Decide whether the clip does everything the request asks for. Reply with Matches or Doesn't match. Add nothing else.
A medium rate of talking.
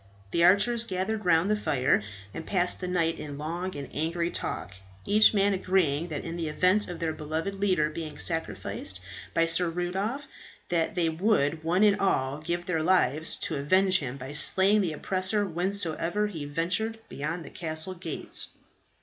Matches